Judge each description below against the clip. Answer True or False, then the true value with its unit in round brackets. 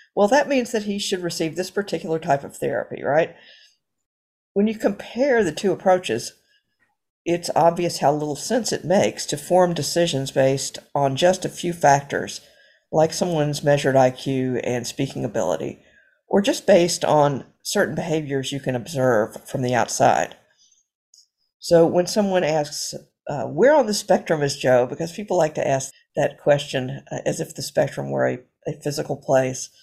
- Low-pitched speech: False (155 Hz)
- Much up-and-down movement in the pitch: False (4.9 semitones)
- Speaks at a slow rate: False (165 wpm)